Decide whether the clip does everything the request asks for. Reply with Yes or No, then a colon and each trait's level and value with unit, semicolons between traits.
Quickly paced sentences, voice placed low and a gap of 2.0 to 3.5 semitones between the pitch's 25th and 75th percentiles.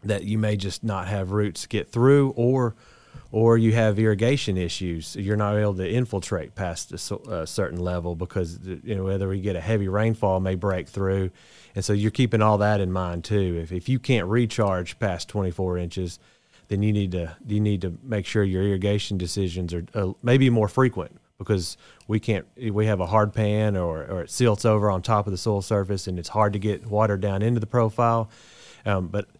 Yes: fast, 210 wpm; low, 105 Hz; average, 2.7 semitones